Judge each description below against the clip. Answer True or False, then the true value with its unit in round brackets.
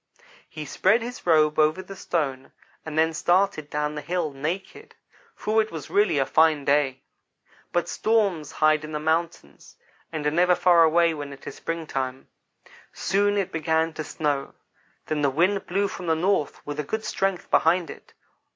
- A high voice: False (160 Hz)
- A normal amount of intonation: True (3.6 semitones)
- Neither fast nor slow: True (175 wpm)